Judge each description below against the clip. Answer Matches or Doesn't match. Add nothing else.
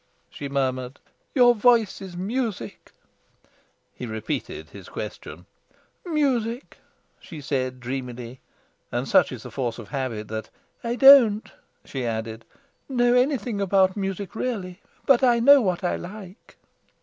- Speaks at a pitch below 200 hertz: Matches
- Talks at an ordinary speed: Doesn't match